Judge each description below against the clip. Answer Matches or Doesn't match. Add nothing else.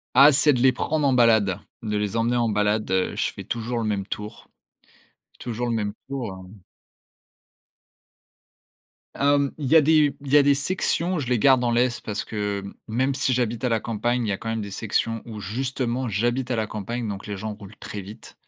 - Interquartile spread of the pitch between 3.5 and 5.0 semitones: Matches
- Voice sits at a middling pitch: Doesn't match